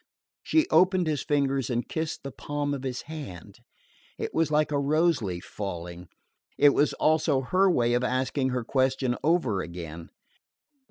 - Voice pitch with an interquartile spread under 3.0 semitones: No, average, 4.4 semitones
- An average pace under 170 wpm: Yes, average, 160 wpm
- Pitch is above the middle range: No, low, 135 Hz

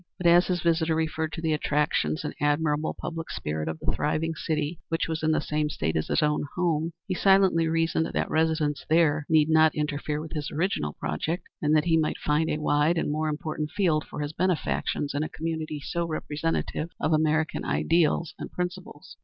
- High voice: No, medium, 155 Hz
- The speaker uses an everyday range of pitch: No, narrow, 1.6 semitones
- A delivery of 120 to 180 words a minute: No, average, 195 wpm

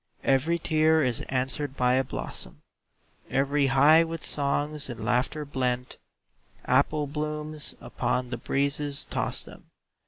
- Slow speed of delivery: Yes, slow, 125 wpm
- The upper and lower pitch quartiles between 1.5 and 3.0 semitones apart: Yes, average, 2.7 semitones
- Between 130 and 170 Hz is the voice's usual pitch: Yes, medium, 140 Hz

